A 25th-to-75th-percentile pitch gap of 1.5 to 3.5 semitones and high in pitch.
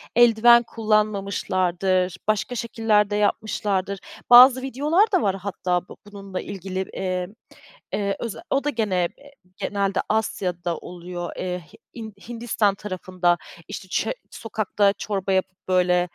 Yes: average, 3.2 semitones; high, 200 Hz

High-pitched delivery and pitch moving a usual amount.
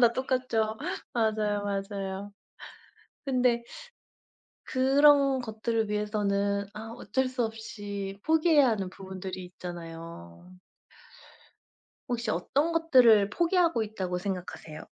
Yes: high, 215 Hz; average, 4.6 semitones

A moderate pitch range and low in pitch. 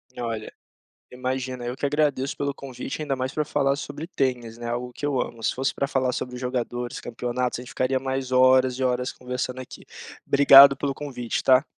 No: narrow, 1.7 semitones; low, 130 Hz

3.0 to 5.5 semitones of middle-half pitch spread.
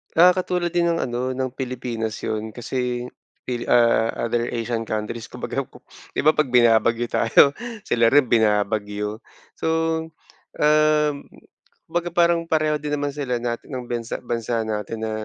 Yes: average, 4.6 semitones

